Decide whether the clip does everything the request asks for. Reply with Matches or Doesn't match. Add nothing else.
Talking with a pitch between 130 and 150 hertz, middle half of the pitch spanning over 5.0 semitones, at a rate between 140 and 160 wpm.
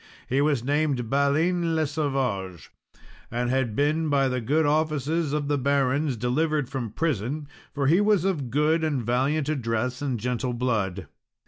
Doesn't match